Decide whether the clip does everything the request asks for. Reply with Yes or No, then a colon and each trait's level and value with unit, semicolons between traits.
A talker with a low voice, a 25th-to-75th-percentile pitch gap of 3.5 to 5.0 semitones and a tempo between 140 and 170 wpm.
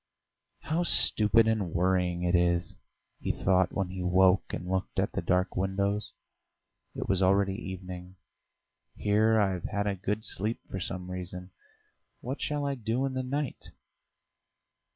No: very low, 95 Hz; average, 3.1 semitones; average, 150 wpm